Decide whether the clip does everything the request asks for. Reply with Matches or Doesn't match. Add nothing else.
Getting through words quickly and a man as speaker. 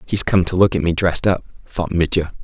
Matches